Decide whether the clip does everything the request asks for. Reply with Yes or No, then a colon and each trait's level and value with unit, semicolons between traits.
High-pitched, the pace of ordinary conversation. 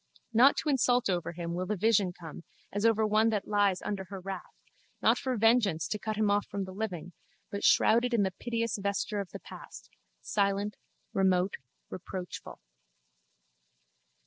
Yes: high, 200 Hz; average, 165 wpm